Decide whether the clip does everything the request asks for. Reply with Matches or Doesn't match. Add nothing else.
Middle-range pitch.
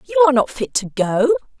Doesn't match